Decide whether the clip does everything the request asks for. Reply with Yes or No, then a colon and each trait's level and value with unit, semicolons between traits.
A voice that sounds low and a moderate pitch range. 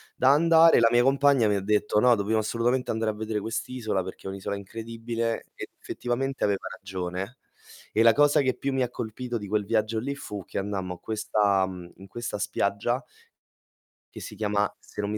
Yes: low, 110 Hz; average, 3.3 semitones